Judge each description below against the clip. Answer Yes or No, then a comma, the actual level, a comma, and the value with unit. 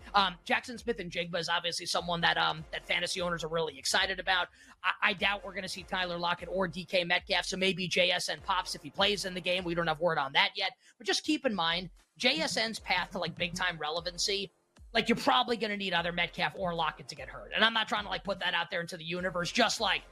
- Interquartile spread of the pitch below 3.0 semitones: Yes, narrow, 2.6 semitones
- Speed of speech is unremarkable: No, fast, 255 wpm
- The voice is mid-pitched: Yes, medium, 180 Hz